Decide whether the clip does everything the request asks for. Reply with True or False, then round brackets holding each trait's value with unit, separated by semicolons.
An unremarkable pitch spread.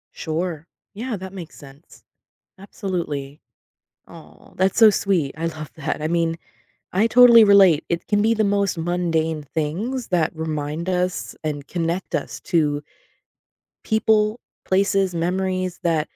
True (3.9 semitones)